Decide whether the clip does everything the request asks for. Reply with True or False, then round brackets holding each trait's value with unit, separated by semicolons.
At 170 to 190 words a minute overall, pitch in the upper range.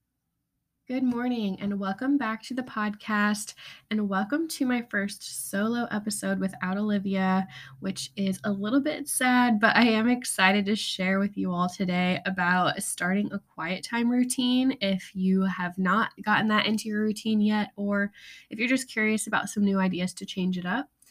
True (175 wpm; 205 Hz)